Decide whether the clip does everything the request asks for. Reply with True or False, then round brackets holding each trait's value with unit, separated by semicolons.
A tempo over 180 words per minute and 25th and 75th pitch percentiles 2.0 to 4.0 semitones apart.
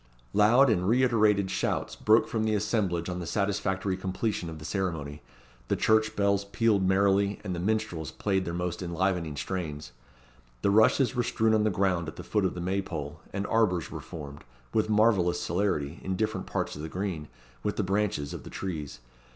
True (190 wpm; 3.6 semitones)